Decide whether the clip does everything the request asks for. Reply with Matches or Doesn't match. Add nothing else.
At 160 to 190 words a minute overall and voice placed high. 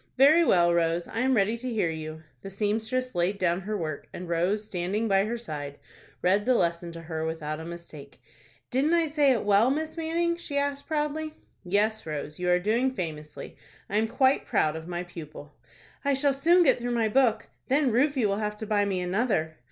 Doesn't match